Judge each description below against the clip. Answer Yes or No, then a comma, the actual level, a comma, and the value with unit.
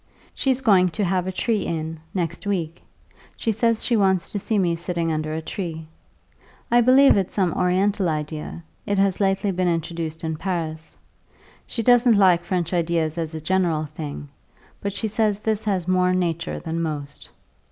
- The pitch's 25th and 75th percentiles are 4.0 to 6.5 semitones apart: No, average, 3.6 semitones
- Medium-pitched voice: Yes, medium, 180 Hz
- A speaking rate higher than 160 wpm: Yes, average, 175 wpm